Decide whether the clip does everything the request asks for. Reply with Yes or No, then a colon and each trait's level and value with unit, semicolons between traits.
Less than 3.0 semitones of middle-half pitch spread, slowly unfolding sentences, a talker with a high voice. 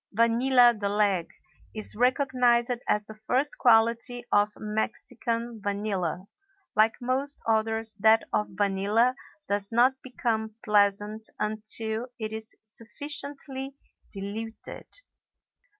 Yes: narrow, 2.5 semitones; slow, 105 wpm; high, 220 Hz